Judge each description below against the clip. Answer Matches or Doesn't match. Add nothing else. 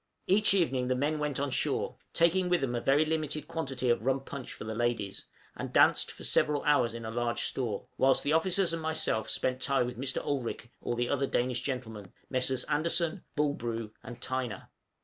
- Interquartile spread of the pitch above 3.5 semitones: Matches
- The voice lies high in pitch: Doesn't match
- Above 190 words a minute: Matches